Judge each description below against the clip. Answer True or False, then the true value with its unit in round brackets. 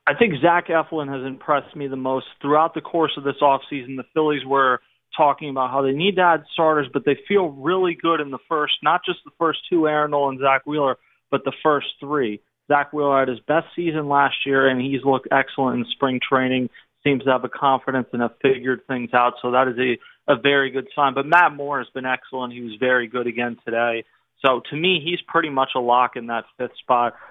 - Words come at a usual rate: False (230 wpm)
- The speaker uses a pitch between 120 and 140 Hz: True (135 Hz)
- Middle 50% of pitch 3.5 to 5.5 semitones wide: False (2.8 semitones)